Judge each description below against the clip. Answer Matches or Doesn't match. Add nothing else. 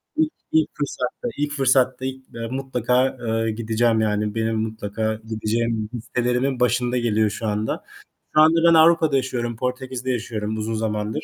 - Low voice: Matches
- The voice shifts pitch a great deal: Doesn't match